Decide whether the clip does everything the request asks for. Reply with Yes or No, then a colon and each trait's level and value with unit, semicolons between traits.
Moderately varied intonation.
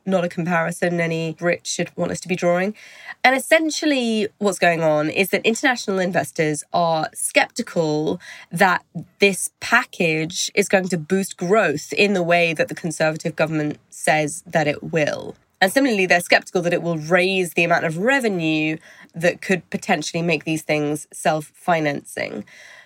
Yes: average, 3.4 semitones